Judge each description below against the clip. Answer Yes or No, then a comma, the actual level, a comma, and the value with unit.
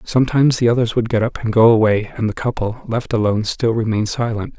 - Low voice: Yes, low, 115 Hz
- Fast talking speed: Yes, fast, 220 wpm